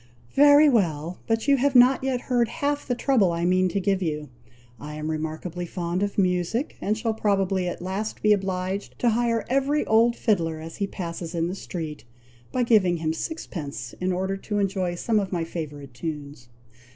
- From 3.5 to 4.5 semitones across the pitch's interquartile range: No, average, 5.3 semitones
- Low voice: No, high, 190 Hz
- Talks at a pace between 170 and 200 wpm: Yes, average, 190 wpm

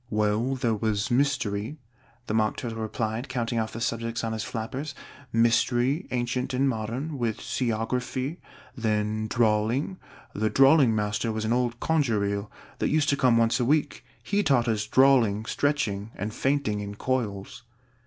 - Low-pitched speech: Yes, low, 115 Hz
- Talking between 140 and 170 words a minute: Yes, average, 155 wpm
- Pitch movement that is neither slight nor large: Yes, average, 3.3 semitones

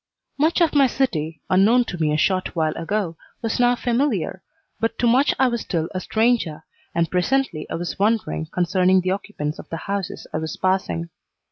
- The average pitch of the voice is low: No, high, 190 Hz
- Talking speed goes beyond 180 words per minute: Yes, average, 190 wpm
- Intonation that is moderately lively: No, wide, 6.3 semitones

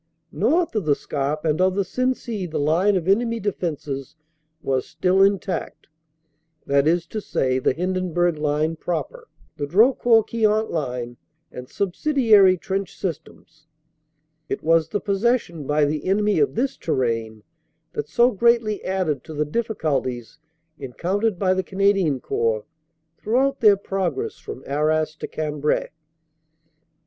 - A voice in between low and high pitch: Yes, medium, 175 Hz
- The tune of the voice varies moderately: No, wide, 5.7 semitones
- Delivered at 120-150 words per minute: Yes, slow, 135 wpm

